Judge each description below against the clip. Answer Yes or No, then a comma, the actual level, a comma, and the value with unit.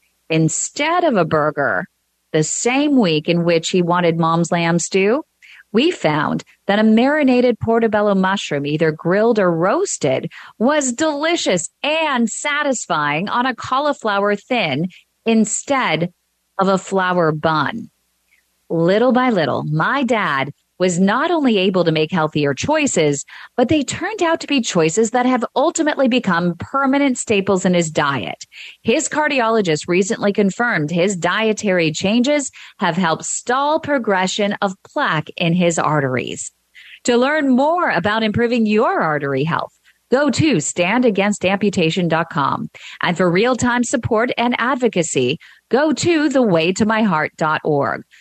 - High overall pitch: Yes, high, 205 Hz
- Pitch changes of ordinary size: No, wide, 6.8 semitones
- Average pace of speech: No, slow, 130 wpm